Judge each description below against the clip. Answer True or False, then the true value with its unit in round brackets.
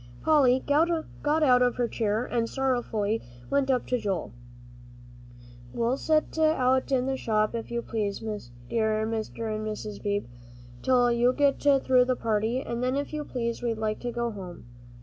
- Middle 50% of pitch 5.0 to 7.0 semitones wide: False (3.3 semitones)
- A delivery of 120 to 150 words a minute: False (170 wpm)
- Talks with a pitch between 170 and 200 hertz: False (245 Hz)